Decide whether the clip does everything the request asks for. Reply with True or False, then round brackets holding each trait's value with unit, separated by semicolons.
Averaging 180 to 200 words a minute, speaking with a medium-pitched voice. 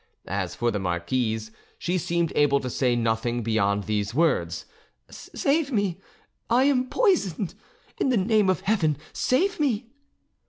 False (145 wpm; 155 Hz)